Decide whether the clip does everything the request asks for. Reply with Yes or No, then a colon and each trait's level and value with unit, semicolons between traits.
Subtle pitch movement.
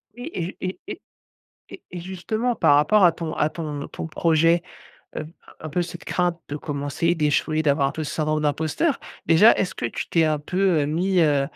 No: average, 3.1 semitones